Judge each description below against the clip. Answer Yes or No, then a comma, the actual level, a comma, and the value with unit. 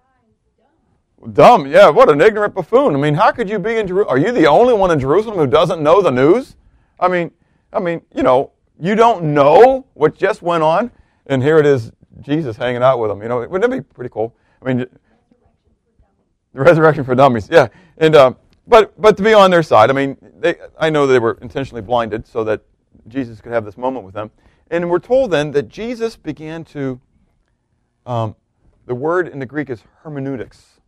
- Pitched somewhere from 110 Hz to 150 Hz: Yes, medium, 140 Hz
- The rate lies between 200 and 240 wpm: Yes, fast, 205 wpm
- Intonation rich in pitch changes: Yes, wide, 6.5 semitones